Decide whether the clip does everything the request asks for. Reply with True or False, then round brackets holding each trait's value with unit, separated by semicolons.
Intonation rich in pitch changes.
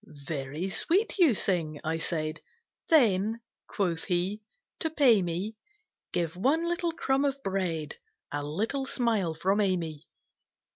True (8.3 semitones)